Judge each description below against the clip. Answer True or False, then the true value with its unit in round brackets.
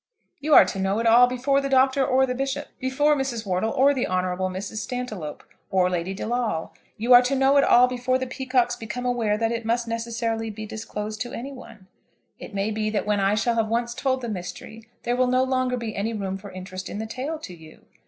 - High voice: True (235 Hz)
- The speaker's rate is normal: False (230 wpm)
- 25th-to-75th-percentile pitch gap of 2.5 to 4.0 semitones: True (3.5 semitones)